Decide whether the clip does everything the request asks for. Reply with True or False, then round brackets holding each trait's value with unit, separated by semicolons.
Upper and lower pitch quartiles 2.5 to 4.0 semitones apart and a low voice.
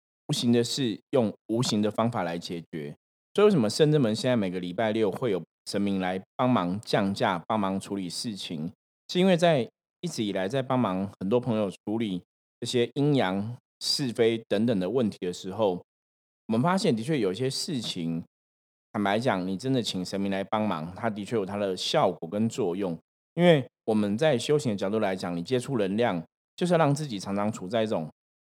False (5.0 semitones; 110 Hz)